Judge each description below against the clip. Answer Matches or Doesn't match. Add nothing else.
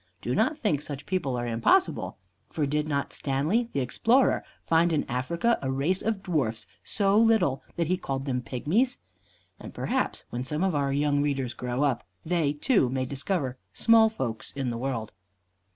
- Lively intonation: Matches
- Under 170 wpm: Doesn't match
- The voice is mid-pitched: Matches